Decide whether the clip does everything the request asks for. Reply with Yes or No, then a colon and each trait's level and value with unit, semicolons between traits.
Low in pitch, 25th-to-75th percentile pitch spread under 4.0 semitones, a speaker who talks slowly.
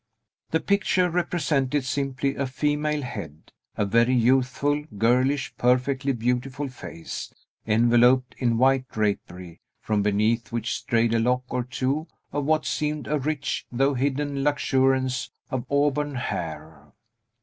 Yes: low, 130 Hz; average, 3.4 semitones; slow, 125 wpm